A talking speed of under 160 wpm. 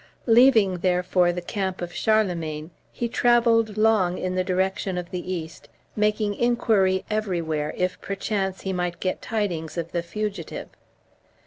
Yes: average, 140 wpm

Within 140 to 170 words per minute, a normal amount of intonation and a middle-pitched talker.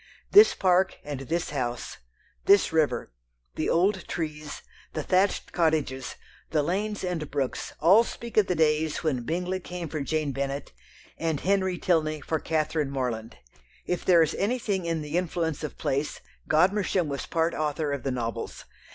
Yes: average, 160 wpm; average, 3.9 semitones; medium, 160 Hz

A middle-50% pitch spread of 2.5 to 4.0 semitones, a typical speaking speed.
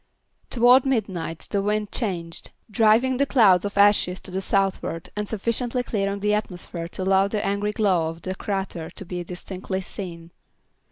Yes: average, 2.8 semitones; average, 165 wpm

